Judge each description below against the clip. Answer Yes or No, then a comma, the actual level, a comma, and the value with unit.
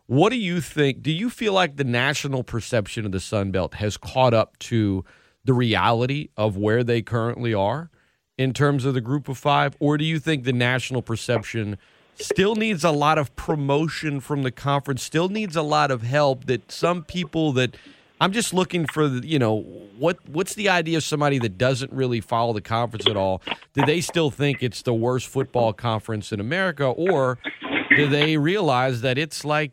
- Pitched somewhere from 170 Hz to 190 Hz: No, low, 135 Hz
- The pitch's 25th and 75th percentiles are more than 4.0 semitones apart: Yes, average, 4.7 semitones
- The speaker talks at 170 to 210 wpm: Yes, average, 200 wpm